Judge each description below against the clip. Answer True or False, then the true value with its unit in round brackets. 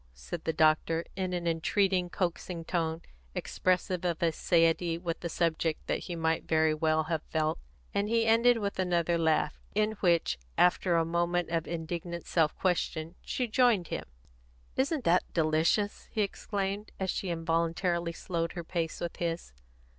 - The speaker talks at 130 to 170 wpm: True (160 wpm)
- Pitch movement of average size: False (2.2 semitones)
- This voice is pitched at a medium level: True (170 Hz)